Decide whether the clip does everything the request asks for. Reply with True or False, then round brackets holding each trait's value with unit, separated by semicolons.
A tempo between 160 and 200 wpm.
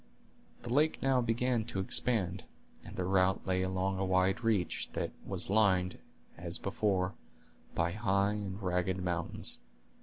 False (145 wpm)